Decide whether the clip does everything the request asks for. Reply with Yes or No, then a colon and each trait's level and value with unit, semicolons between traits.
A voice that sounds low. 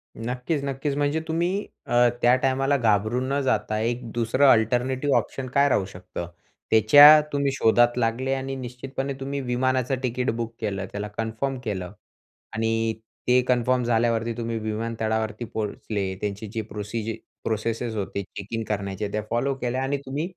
Yes: low, 120 Hz